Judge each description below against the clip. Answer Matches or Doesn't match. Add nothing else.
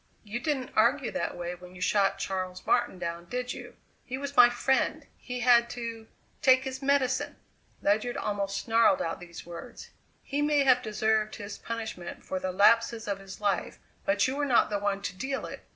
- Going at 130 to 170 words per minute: Doesn't match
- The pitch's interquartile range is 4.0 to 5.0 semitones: Matches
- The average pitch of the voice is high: Matches